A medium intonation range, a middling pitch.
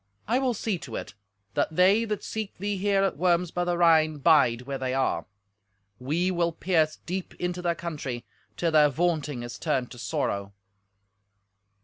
Yes: average, 4.5 semitones; medium, 170 Hz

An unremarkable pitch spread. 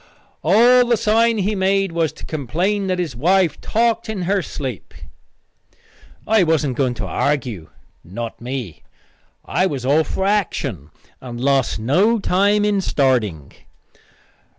No: wide, 7.9 semitones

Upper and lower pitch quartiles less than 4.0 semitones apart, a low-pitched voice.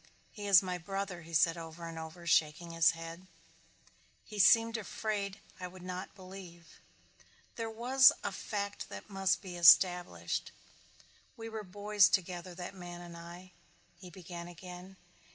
No: average, 2.7 semitones; medium, 180 Hz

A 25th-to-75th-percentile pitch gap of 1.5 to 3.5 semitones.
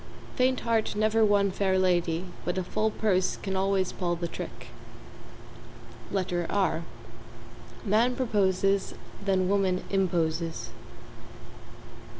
Yes: narrow, 2.5 semitones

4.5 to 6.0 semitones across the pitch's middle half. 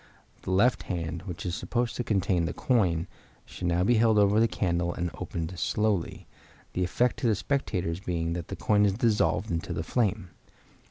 No: average, 4.1 semitones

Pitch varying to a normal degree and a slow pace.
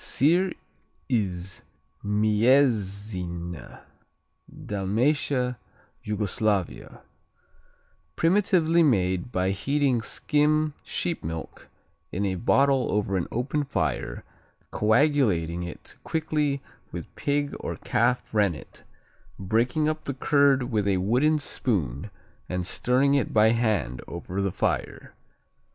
No: wide, 7.0 semitones; slow, 100 wpm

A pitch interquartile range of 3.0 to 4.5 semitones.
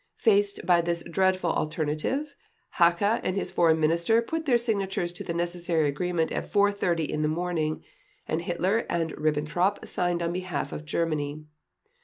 Yes: average, 3.3 semitones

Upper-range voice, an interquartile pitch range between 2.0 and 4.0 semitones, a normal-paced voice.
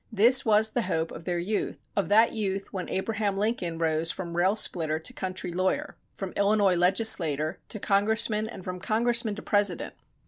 Yes: high, 195 Hz; average, 3.6 semitones; average, 175 wpm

